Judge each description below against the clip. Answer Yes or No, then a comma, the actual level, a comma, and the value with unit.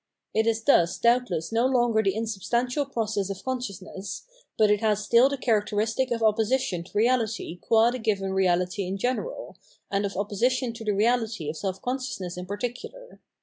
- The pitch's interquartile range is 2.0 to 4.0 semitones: Yes, average, 3.7 semitones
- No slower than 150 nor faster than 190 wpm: Yes, average, 185 wpm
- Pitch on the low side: No, high, 220 Hz